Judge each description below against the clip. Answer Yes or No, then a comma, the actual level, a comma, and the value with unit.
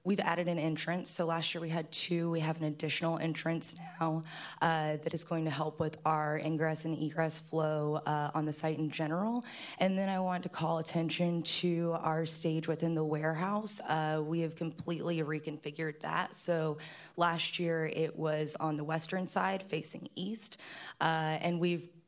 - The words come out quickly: No, average, 180 wpm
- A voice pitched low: No, medium, 160 Hz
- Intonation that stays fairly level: Yes, narrow, 1.5 semitones